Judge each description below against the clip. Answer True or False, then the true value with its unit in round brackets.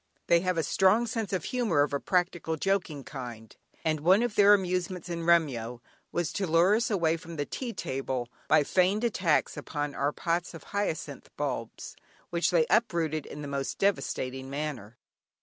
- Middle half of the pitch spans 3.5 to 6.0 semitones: True (4.8 semitones)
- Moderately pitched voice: True (165 Hz)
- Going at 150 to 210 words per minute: True (175 wpm)